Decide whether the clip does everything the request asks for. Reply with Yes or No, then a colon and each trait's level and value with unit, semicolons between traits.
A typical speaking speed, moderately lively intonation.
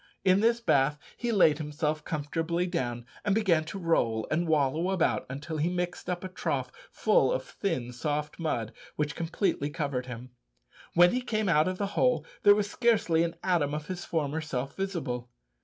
Yes: average, 180 wpm; average, 4.4 semitones